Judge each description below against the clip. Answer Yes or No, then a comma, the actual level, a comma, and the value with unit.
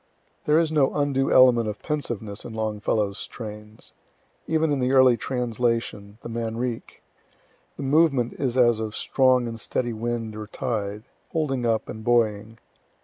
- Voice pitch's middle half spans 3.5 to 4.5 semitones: No, average, 3.1 semitones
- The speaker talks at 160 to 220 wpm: No, average, 145 wpm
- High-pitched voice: No, low, 120 Hz